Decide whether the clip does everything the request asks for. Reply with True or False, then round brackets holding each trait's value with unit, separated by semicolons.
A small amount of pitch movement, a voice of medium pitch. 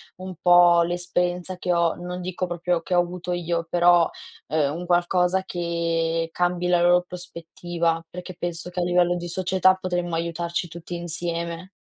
True (0.8 semitones; 175 Hz)